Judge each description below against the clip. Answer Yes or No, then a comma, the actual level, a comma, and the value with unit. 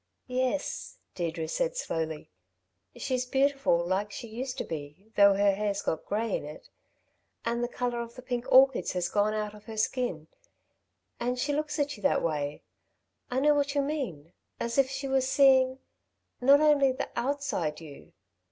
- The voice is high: Yes, high, 240 Hz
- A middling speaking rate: Yes, average, 170 wpm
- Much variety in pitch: Yes, wide, 5.8 semitones